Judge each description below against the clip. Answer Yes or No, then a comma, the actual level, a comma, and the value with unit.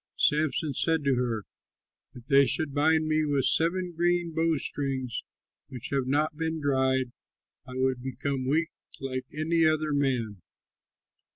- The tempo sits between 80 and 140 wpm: Yes, slow, 135 wpm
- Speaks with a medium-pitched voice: Yes, medium, 145 Hz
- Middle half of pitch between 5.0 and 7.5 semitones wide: No, average, 3.3 semitones